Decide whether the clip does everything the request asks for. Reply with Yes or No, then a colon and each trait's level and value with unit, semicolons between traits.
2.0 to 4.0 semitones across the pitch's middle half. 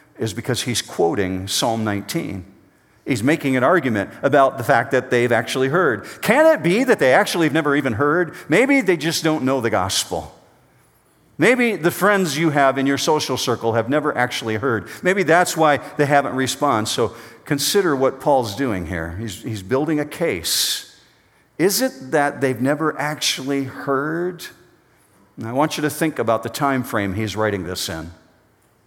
No: average, 5.1 semitones